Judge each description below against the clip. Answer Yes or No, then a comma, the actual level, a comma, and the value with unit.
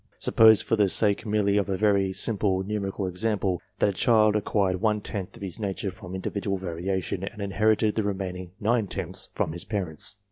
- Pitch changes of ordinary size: No, narrow, 2.1 semitones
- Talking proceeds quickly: No, average, 185 wpm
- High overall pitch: No, low, 100 Hz